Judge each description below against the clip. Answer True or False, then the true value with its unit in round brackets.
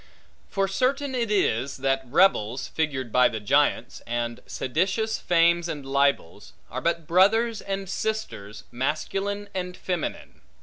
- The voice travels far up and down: True (6.9 semitones)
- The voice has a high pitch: False (170 Hz)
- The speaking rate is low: True (130 wpm)